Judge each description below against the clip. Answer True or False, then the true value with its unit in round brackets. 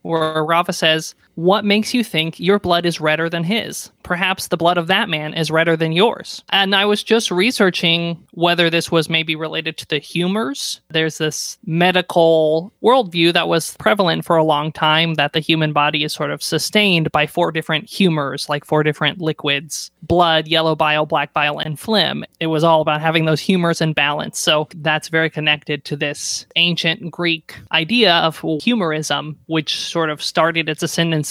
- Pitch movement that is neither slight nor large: False (2.0 semitones)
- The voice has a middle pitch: True (160 Hz)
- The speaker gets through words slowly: False (185 wpm)